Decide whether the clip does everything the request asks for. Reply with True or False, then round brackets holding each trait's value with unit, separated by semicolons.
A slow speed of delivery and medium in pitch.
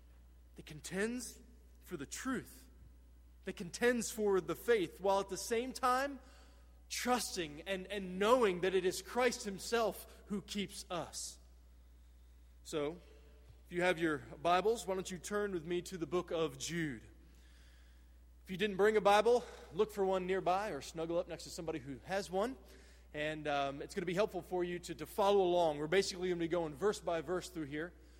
False (185 wpm; 175 Hz)